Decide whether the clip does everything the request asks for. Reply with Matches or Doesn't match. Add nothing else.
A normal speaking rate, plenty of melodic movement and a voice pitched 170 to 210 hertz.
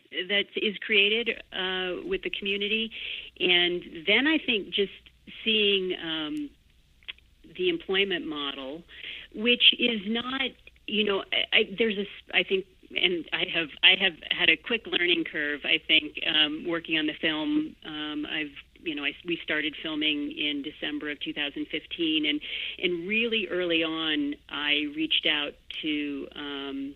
Matches